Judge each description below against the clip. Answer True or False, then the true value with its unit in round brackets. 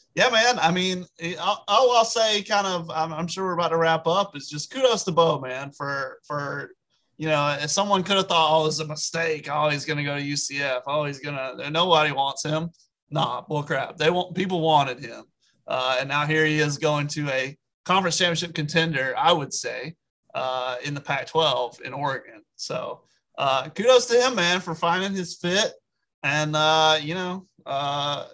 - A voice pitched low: False (155 Hz)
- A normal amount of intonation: True (3.7 semitones)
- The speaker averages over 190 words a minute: True (200 wpm)